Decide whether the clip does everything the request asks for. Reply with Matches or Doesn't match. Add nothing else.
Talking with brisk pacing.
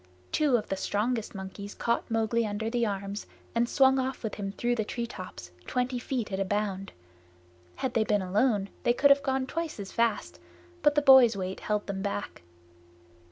Doesn't match